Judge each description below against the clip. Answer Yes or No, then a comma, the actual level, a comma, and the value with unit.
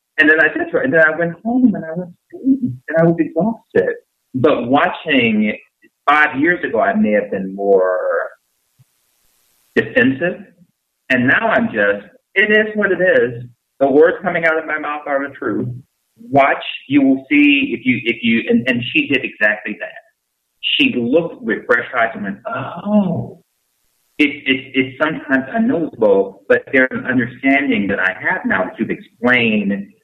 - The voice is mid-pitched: Yes, medium, 160 Hz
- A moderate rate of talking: Yes, average, 170 wpm